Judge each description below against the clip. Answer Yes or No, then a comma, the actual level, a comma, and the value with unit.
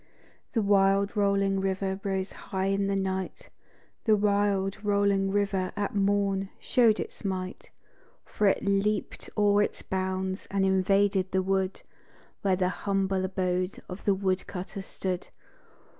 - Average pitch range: No, narrow, 1.1 semitones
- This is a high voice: Yes, high, 195 Hz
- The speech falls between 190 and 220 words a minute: No, average, 140 wpm